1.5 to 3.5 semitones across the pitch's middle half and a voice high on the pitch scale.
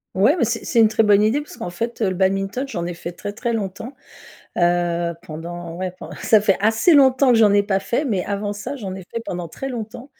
No: average, 4.2 semitones; high, 205 Hz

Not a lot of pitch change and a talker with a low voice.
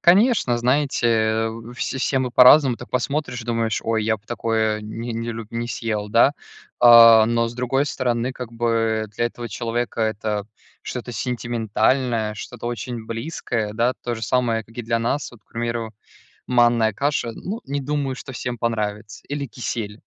Yes: narrow, 2.0 semitones; low, 115 Hz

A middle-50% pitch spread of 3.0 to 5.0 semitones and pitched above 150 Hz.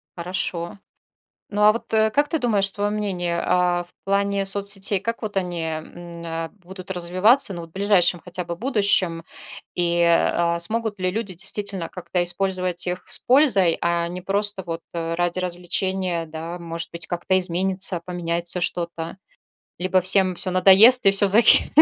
No: narrow, 2.6 semitones; medium, 185 Hz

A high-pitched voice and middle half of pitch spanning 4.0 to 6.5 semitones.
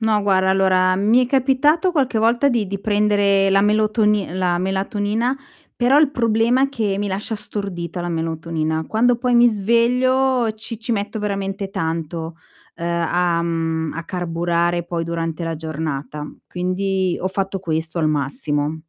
Yes: high, 195 Hz; average, 4.8 semitones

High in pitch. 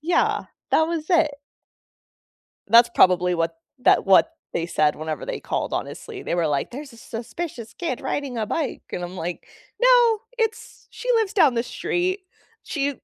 Yes: very high, 260 Hz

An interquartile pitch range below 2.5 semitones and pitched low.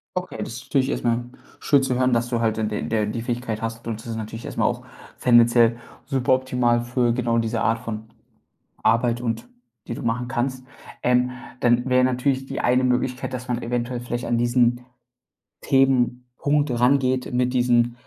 Yes: narrow, 1.4 semitones; low, 120 Hz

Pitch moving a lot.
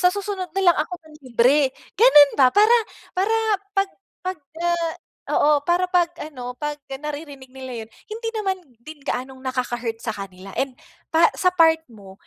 Yes: wide, 6.0 semitones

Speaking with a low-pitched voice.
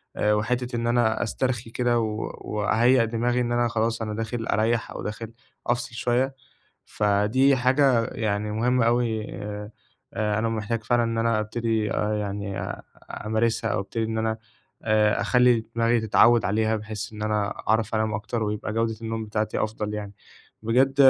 Yes: low, 110 Hz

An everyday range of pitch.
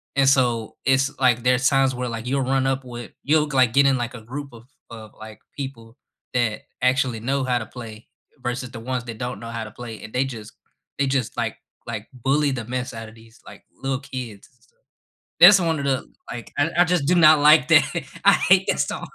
Yes: average, 3.0 semitones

